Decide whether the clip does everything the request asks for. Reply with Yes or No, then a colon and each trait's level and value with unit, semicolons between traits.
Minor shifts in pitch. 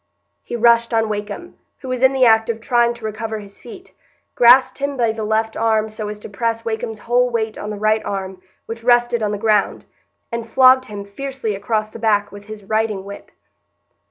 Yes: narrow, 2.1 semitones